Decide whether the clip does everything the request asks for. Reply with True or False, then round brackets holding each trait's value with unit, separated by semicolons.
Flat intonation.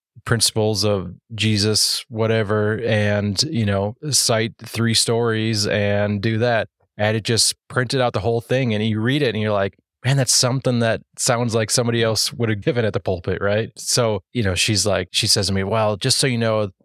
True (2.3 semitones)